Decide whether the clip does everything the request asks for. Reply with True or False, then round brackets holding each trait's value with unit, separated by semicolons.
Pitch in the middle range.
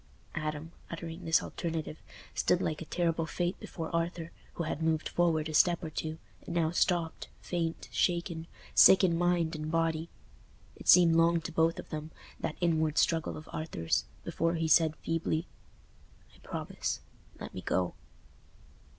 True (165 Hz)